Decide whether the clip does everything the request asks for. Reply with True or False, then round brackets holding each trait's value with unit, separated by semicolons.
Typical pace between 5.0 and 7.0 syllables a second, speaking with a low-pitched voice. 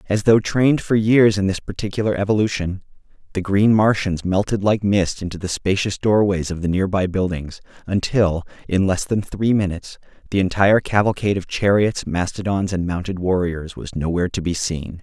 True (5.3 syllables/s; 95 Hz)